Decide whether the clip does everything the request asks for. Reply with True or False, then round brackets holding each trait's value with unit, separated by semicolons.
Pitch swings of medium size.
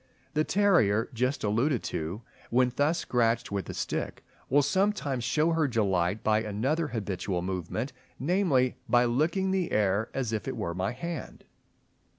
False (6.5 semitones)